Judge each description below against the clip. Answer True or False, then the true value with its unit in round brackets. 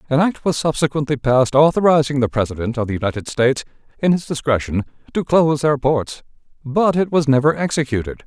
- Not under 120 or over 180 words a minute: True (175 wpm)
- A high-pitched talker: False (140 Hz)